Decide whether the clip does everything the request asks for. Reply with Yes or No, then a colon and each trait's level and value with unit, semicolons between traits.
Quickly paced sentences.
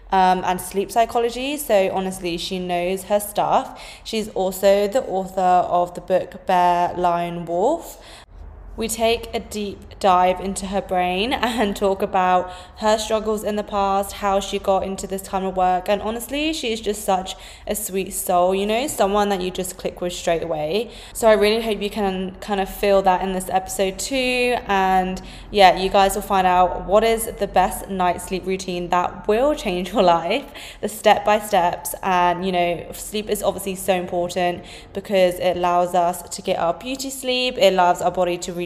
No: average, 190 wpm